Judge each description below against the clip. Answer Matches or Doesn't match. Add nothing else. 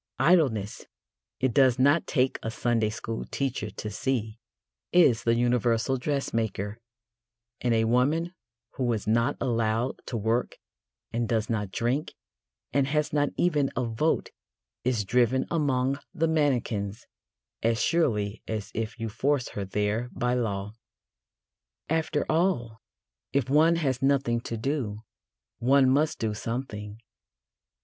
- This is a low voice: Matches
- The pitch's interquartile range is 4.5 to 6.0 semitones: Doesn't match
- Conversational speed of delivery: Doesn't match